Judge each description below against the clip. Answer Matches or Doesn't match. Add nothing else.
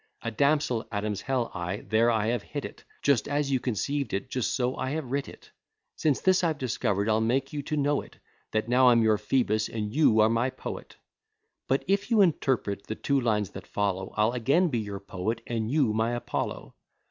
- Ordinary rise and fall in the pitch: Matches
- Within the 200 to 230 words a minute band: Matches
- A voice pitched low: Matches